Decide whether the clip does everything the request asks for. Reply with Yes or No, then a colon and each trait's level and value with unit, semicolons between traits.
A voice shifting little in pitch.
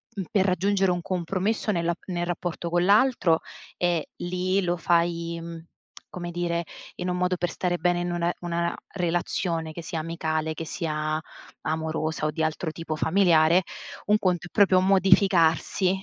Yes: narrow, 1.8 semitones